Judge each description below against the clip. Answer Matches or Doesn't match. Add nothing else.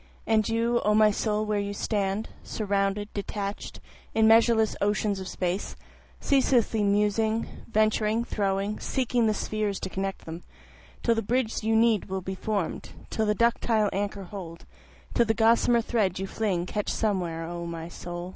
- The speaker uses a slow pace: Doesn't match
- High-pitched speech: Matches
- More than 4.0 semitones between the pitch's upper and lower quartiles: Doesn't match